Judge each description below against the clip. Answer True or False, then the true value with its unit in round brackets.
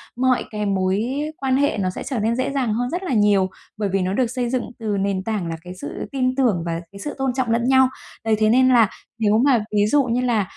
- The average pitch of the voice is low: False (230 Hz)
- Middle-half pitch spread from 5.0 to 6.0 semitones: False (4.2 semitones)